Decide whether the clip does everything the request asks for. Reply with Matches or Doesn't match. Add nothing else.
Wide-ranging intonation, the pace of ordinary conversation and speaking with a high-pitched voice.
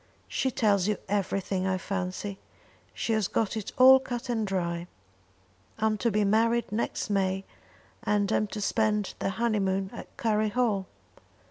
Doesn't match